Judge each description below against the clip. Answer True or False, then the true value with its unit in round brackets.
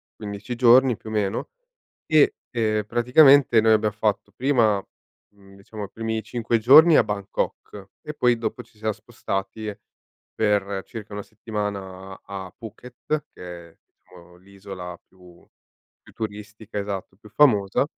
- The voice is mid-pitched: False (105 Hz)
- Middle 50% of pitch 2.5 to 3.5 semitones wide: True (2.8 semitones)